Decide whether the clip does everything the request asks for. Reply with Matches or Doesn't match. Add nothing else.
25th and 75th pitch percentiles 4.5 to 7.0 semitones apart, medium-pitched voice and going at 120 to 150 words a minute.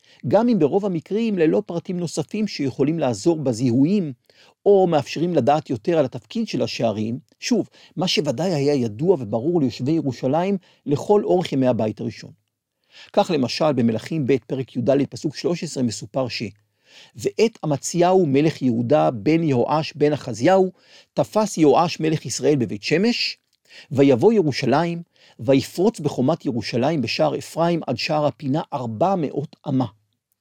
Matches